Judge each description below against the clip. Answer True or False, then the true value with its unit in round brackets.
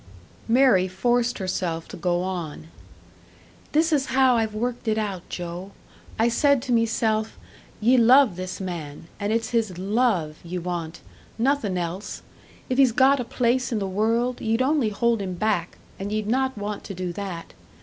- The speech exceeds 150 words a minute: True (170 wpm)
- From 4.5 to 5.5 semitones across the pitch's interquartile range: True (4.8 semitones)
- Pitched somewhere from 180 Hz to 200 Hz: False (215 Hz)